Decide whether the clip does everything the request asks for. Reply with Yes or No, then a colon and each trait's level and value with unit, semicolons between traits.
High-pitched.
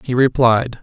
No: low, 125 Hz